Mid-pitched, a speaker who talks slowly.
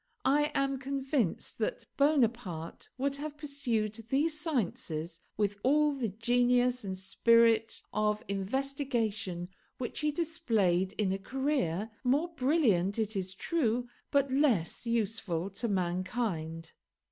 No: high, 230 Hz; slow, 120 wpm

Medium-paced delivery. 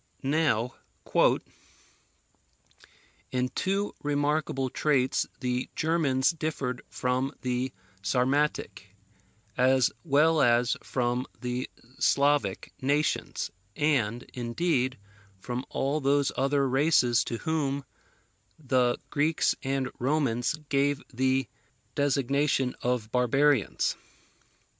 No: slow, 85 wpm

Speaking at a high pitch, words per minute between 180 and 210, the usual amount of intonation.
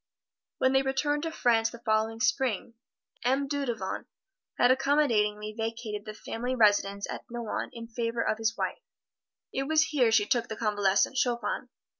No: high, 235 Hz; average, 155 wpm; average, 3.4 semitones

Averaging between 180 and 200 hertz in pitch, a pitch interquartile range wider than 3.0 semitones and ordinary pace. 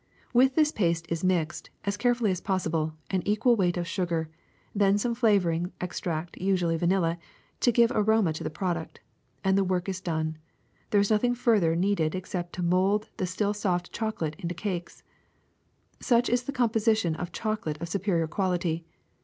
Yes: medium, 185 Hz; average, 3.9 semitones; average, 170 wpm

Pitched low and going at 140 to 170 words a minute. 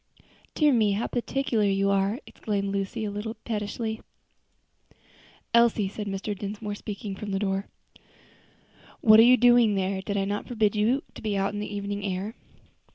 No: high, 205 Hz; average, 165 wpm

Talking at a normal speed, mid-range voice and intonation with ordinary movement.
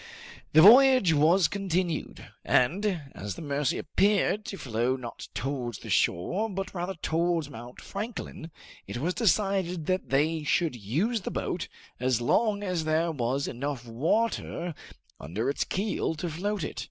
No: average, 150 wpm; medium, 165 Hz; wide, 6.4 semitones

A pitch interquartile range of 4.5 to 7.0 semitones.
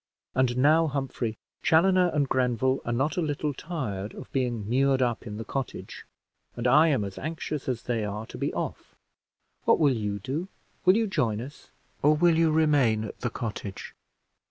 Yes: average, 5.0 semitones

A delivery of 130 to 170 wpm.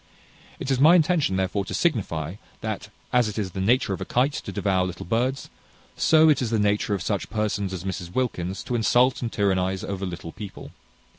No: fast, 205 wpm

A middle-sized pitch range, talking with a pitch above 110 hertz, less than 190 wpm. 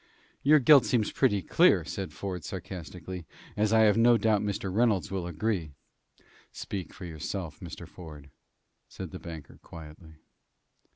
No: average, 4.7 semitones; very low, 95 Hz; average, 140 wpm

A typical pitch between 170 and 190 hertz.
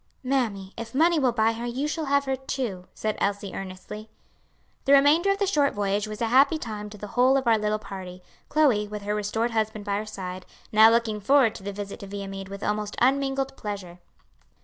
No: high, 215 Hz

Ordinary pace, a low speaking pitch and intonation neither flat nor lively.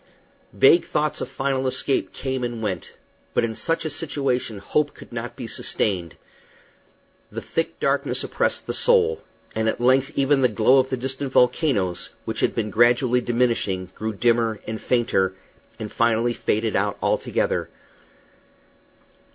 Yes: average, 150 wpm; low, 120 Hz; average, 3.5 semitones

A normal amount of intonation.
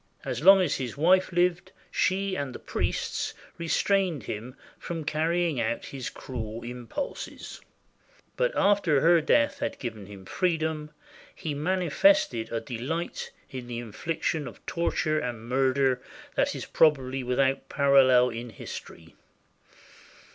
No: wide, 5.8 semitones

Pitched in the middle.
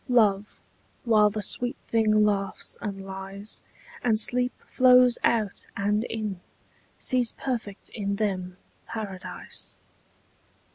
No: high, 215 Hz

